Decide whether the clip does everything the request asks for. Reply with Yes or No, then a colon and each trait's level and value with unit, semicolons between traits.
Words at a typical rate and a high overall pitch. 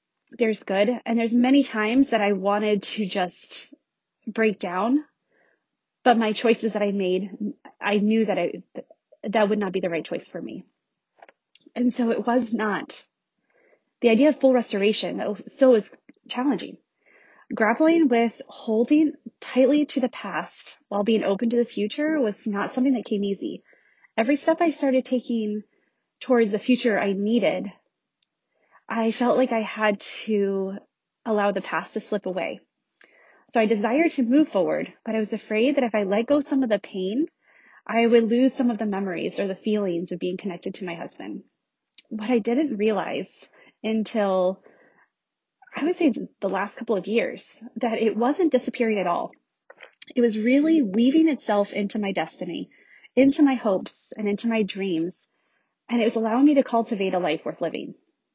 Yes: average, 170 wpm; high, 225 Hz